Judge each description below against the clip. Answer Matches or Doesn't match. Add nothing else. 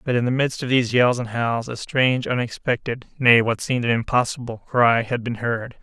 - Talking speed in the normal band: Matches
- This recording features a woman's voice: Doesn't match